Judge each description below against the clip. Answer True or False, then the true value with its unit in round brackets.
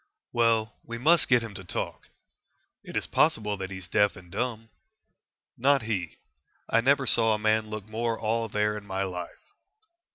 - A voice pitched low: True (110 Hz)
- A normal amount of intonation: False (2.3 semitones)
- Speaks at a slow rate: False (175 wpm)